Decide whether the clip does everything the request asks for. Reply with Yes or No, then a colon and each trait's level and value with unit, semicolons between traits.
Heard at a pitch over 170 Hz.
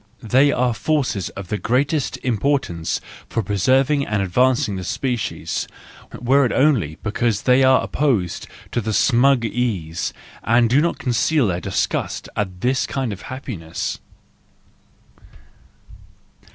No: low, 120 Hz